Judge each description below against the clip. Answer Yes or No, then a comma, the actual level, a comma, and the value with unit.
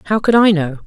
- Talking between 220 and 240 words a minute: No, fast, 275 wpm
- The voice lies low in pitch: No, high, 190 Hz